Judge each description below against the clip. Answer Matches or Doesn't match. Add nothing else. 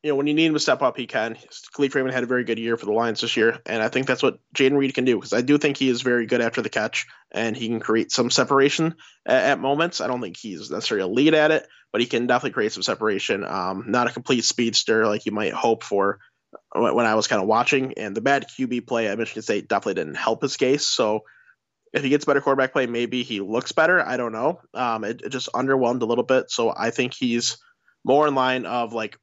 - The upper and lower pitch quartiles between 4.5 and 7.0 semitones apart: Doesn't match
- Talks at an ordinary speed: Doesn't match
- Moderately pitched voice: Doesn't match